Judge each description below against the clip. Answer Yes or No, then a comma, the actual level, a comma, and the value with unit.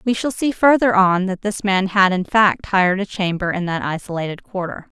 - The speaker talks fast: Yes, fast, 215 wpm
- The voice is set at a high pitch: Yes, high, 195 Hz